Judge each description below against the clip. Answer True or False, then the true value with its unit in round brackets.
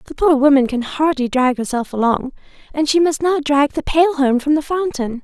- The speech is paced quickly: True (220 wpm)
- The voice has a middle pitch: False (285 Hz)